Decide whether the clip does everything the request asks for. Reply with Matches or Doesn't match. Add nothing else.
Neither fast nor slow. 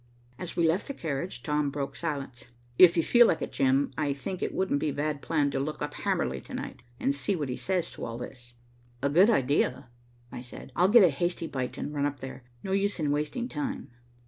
Doesn't match